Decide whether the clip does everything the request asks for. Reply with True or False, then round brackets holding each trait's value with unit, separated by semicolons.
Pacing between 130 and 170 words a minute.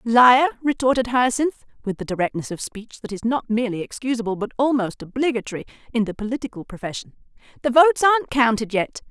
True (165 wpm)